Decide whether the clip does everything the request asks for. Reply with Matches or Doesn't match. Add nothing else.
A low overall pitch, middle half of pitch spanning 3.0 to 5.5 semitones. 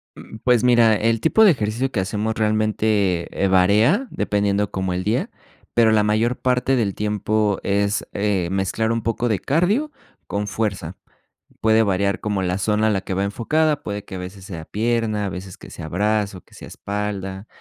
Doesn't match